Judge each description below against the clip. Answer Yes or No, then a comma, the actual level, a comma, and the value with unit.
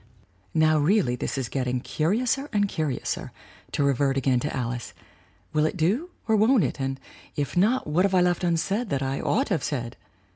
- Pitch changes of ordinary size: No, wide, 7.0 semitones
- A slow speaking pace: No, average, 195 wpm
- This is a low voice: No, medium, 155 Hz